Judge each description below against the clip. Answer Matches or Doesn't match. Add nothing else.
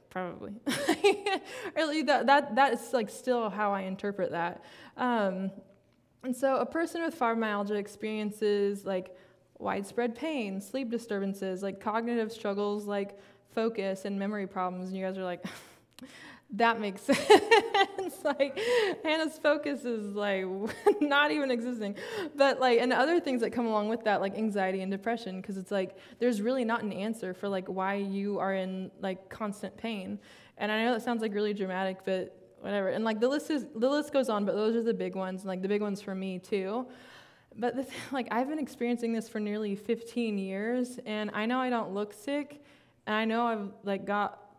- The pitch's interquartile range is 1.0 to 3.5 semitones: Doesn't match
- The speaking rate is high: Doesn't match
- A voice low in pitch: Doesn't match